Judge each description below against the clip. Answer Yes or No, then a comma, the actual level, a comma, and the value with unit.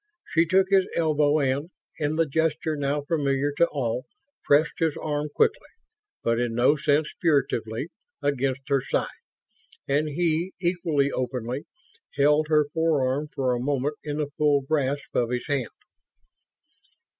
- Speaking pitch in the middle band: Yes, medium, 145 Hz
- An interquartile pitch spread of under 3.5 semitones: Yes, narrow, 2.6 semitones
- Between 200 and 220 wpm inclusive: No, average, 145 wpm